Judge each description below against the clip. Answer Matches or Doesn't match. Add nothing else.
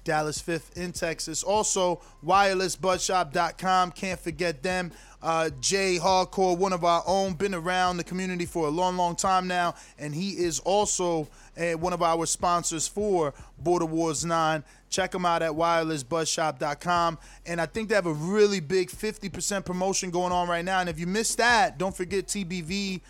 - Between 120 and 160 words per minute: Doesn't match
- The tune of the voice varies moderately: Doesn't match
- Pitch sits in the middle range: Matches